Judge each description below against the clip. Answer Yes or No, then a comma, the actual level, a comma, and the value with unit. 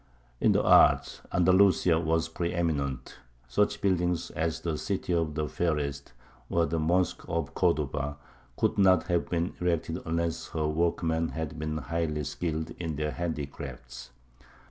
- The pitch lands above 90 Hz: No, very low, 80 Hz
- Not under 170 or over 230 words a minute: No, average, 145 wpm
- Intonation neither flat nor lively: No, narrow, 2.3 semitones